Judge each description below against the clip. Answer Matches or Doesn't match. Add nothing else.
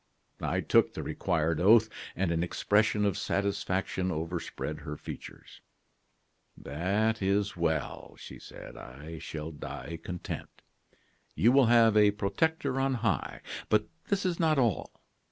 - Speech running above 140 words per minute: Doesn't match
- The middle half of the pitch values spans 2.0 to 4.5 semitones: Doesn't match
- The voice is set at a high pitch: Doesn't match